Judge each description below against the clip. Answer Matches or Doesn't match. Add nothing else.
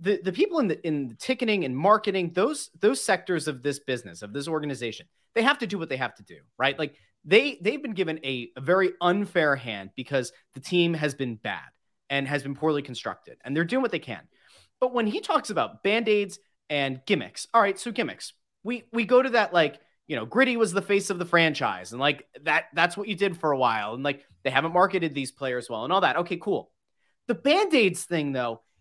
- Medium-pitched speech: Matches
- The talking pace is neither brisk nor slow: Doesn't match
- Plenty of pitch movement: Matches